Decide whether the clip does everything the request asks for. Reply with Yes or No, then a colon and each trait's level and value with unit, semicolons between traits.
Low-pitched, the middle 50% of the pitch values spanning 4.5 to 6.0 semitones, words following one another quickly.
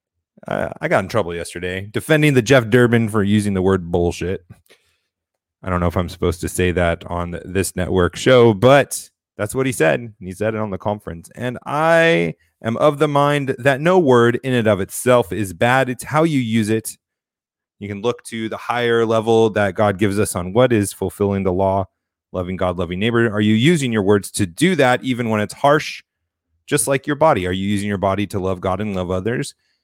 Yes: low, 105 Hz; average, 4.9 semitones; fast, 215 wpm